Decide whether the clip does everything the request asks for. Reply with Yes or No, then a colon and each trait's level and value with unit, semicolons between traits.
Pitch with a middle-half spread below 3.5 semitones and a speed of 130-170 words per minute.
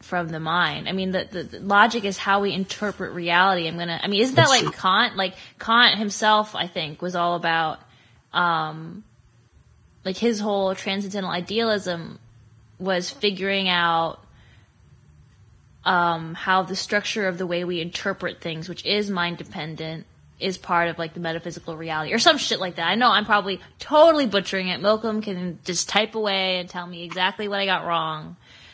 No: average, 2.9 semitones; average, 180 wpm